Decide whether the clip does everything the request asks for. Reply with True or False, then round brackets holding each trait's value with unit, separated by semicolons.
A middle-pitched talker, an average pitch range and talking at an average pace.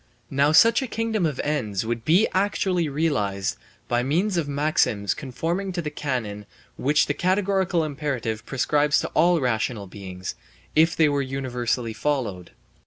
False (145 Hz; 6.1 semitones; 150 wpm)